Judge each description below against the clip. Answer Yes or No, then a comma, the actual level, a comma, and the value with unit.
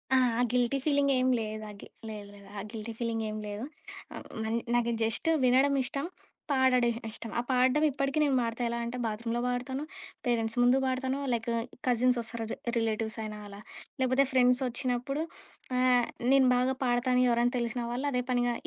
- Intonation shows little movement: Yes, narrow, 2.1 semitones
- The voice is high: Yes, high, 245 Hz